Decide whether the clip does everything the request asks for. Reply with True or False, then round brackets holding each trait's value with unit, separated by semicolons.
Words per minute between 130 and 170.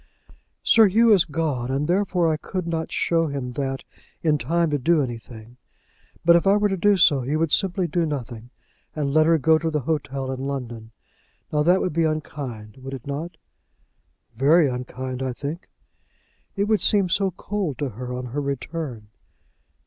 False (180 wpm)